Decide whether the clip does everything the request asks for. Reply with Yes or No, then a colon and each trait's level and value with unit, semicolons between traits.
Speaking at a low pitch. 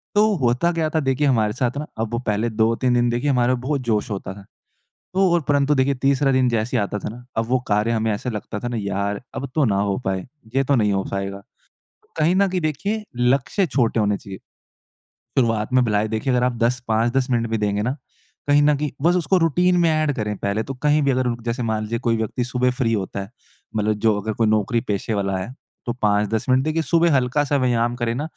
Yes: low, 120 Hz